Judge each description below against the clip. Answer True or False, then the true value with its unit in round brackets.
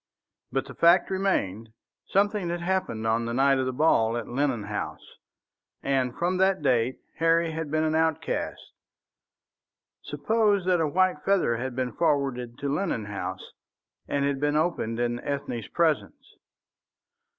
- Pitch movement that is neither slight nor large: False (6.1 semitones)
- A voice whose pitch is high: False (145 Hz)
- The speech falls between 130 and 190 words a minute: True (150 wpm)